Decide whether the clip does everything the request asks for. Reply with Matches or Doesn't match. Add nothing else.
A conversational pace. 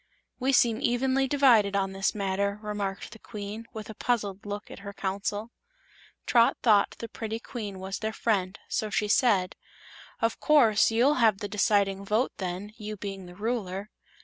Matches